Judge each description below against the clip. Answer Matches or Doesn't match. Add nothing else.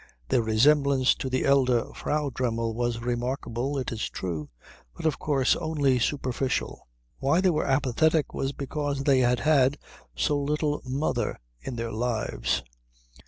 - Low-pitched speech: Matches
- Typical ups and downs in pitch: Matches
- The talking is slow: Doesn't match